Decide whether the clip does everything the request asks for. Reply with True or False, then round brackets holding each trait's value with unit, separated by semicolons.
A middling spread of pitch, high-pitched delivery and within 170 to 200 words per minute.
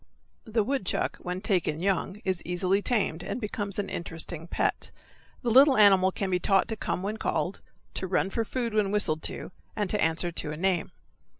True (3.1 semitones; 195 Hz; 190 wpm)